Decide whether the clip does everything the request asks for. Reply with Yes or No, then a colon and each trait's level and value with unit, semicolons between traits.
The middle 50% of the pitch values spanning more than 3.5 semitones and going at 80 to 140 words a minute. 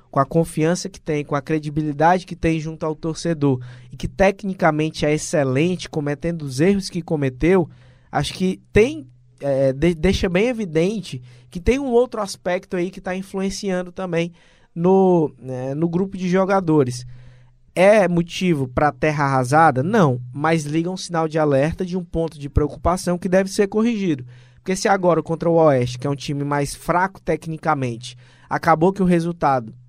No: average, 4.4 semitones; average, 170 wpm